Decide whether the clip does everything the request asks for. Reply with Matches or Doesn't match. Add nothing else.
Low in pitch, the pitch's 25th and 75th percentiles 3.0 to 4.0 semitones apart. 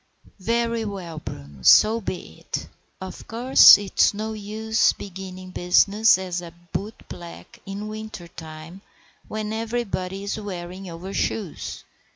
Doesn't match